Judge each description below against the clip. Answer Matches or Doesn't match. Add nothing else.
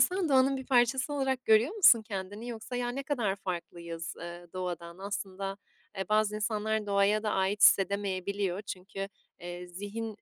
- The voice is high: Matches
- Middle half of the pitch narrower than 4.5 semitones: Matches